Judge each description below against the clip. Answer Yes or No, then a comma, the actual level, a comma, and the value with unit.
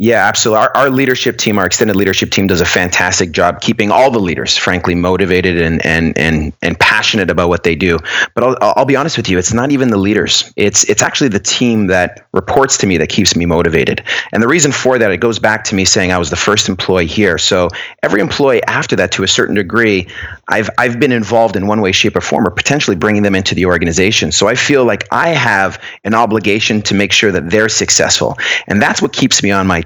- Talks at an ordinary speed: No, fast, 235 wpm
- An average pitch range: Yes, average, 3.2 semitones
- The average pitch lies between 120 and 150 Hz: No, low, 100 Hz